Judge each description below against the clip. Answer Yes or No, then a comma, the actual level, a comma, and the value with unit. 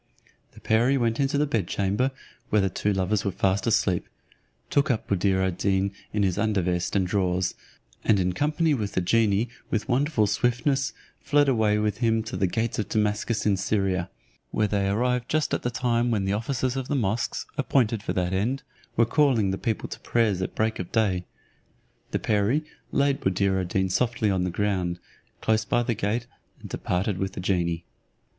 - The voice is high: No, low, 105 Hz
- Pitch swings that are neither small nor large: Yes, average, 4.0 semitones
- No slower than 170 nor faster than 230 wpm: Yes, average, 190 wpm